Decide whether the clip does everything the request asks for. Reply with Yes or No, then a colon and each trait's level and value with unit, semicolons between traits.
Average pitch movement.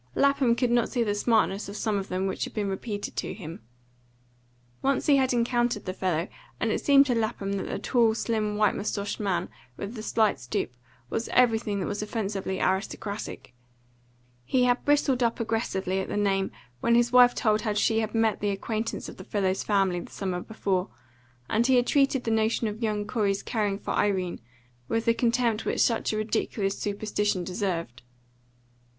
Yes: average, 3.1 semitones